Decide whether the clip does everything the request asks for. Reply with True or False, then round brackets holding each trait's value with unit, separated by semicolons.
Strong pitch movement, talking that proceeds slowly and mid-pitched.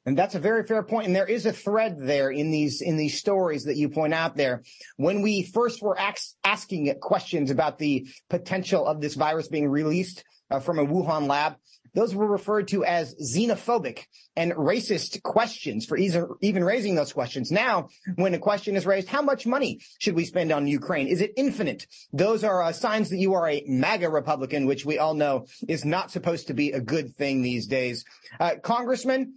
False (6.0 semitones; 205 wpm; 175 Hz)